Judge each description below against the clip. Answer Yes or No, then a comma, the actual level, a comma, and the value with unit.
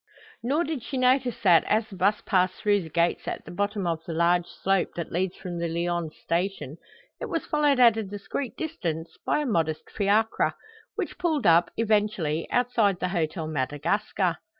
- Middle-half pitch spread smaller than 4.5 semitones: No, average, 4.9 semitones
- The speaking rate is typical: Yes, average, 180 wpm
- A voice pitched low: No, high, 190 Hz